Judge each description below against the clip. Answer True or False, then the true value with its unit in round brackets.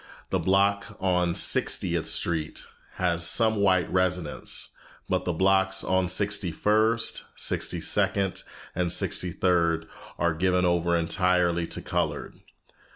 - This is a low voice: True (90 Hz)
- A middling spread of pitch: False (2.0 semitones)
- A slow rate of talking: True (120 wpm)